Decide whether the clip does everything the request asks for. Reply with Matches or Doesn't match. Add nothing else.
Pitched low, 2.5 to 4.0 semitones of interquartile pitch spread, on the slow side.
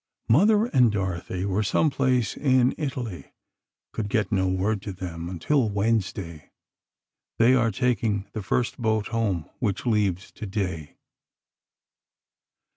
Doesn't match